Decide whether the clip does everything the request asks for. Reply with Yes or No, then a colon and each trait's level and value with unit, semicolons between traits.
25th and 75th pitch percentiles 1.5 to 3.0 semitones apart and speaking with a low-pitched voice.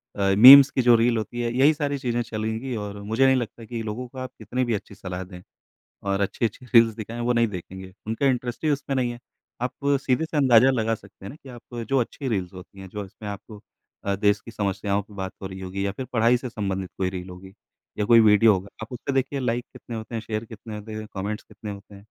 No: average, 3.7 semitones; low, 110 Hz